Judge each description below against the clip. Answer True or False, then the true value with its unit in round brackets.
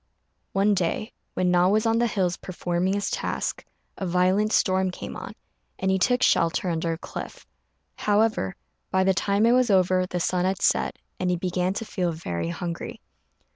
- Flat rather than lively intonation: True (2.3 semitones)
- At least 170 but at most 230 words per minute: True (180 wpm)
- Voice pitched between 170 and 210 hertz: True (185 Hz)